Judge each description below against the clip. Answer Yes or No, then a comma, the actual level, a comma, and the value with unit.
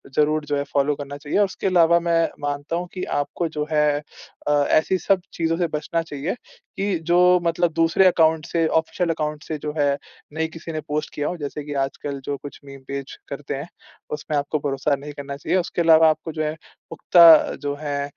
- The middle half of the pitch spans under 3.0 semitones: Yes, narrow, 2.6 semitones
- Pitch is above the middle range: No, medium, 155 Hz